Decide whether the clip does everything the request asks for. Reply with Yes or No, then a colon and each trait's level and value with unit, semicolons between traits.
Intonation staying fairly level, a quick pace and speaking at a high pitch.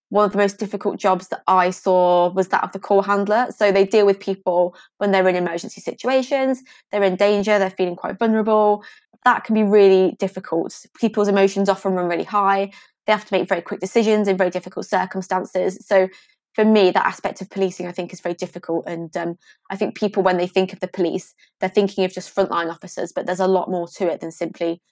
Yes: narrow, 2.2 semitones; fast, 220 wpm; high, 195 Hz